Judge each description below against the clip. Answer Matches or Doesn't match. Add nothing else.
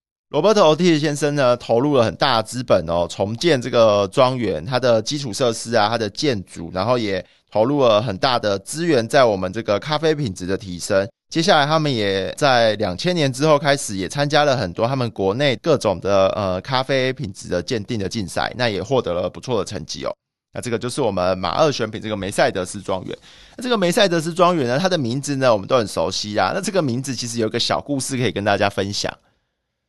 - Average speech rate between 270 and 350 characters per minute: Matches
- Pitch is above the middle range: Doesn't match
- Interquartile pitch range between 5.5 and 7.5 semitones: Matches